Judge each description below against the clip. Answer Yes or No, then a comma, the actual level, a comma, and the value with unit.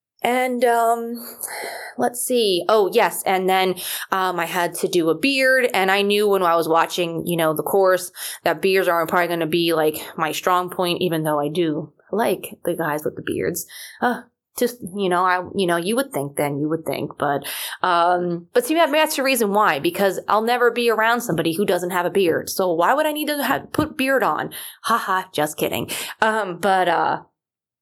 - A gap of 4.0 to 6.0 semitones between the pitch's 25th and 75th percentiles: Yes, average, 5.3 semitones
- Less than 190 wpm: No, fast, 205 wpm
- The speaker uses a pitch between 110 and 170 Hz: No, medium, 185 Hz